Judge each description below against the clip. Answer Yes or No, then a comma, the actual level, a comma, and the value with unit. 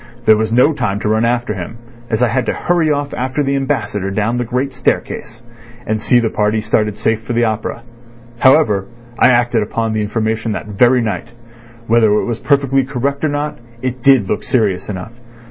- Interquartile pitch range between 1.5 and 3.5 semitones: Yes, average, 3.2 semitones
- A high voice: No, low, 115 Hz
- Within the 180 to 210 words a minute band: Yes, average, 195 wpm